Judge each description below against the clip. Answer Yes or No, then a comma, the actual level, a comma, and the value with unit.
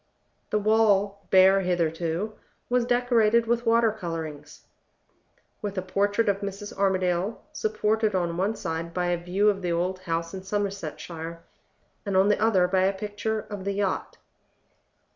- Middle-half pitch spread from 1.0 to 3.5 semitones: Yes, average, 2.9 semitones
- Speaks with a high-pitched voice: Yes, high, 195 Hz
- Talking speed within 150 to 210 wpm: Yes, average, 155 wpm